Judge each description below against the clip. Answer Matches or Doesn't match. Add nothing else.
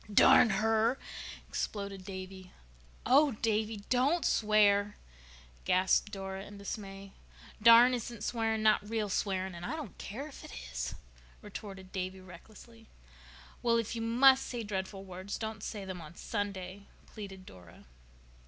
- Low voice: Doesn't match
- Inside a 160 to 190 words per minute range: Doesn't match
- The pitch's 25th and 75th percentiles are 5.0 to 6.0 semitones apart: Doesn't match